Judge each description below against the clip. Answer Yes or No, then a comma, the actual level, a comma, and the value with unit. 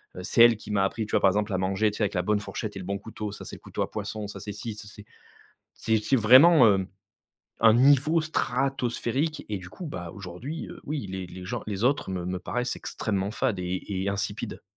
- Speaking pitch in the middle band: No, low, 105 Hz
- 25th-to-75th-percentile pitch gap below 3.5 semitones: No, average, 4.2 semitones